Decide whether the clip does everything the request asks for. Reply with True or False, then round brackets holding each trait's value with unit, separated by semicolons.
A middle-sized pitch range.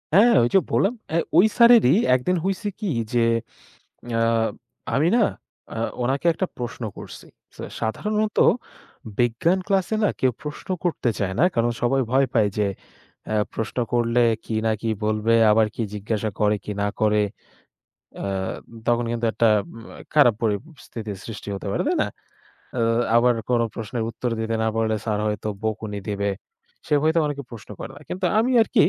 False (6.2 semitones)